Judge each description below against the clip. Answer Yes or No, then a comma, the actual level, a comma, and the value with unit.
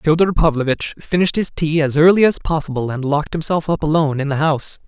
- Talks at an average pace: No, fast, 210 wpm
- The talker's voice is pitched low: No, medium, 155 Hz